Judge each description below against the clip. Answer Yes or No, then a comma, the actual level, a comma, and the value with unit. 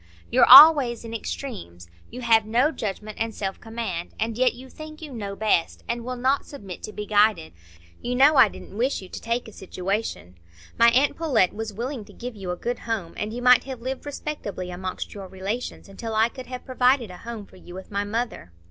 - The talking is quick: Yes, fast, 215 wpm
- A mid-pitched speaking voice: No, high, 225 Hz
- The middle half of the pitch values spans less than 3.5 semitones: No, average, 4.1 semitones